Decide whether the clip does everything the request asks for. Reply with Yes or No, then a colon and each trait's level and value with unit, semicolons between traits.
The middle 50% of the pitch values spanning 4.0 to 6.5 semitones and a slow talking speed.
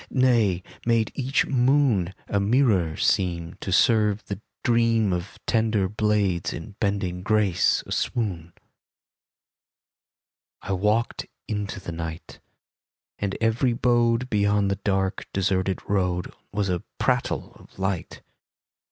No: average, 3.5 semitones; slow, 115 wpm